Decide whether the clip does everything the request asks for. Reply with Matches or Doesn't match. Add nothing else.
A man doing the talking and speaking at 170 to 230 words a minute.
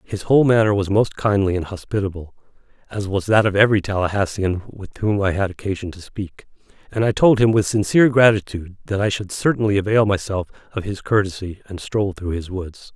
Matches